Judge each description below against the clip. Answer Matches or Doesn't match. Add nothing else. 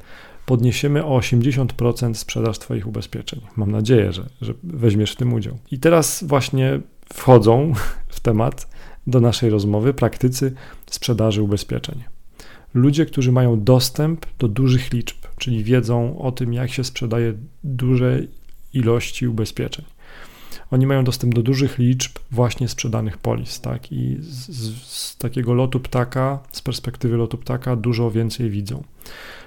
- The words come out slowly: Doesn't match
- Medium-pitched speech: Doesn't match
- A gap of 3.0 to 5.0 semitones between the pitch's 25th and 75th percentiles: Doesn't match